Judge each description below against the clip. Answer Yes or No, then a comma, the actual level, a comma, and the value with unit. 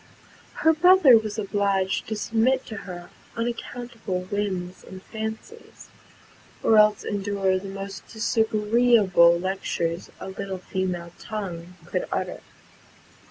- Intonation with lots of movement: No, average, 3.0 semitones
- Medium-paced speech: No, slow, 115 wpm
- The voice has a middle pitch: No, high, 200 Hz